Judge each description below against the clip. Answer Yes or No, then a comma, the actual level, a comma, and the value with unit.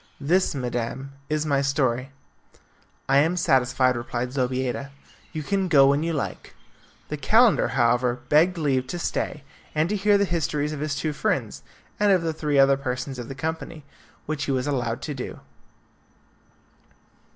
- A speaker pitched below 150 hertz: Yes, medium, 140 Hz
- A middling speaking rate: Yes, average, 160 wpm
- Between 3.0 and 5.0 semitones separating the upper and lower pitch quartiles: Yes, average, 3.7 semitones